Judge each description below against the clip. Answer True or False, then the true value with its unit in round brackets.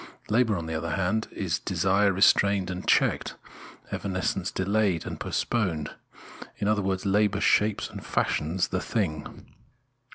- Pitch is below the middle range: True (95 Hz)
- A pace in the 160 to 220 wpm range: False (135 wpm)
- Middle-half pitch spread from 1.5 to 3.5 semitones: True (2.5 semitones)